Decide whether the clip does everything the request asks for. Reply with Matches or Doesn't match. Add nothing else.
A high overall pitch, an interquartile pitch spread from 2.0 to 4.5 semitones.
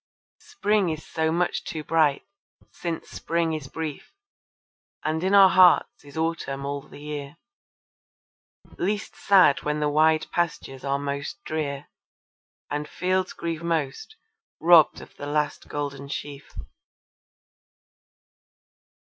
Doesn't match